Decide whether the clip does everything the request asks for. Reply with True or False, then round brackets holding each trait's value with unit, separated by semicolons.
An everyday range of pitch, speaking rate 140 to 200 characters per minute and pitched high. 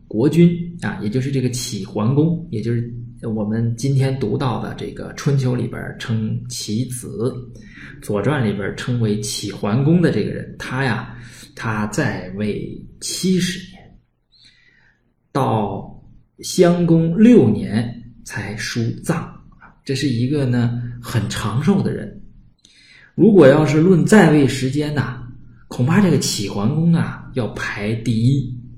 False (4.9 semitones; 190 characters per minute; 125 Hz)